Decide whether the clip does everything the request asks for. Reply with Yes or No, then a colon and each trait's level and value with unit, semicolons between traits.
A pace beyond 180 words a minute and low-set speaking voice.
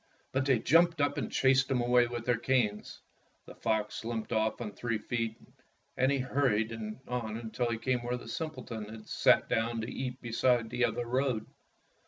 Yes: average, 190 wpm; low, 120 Hz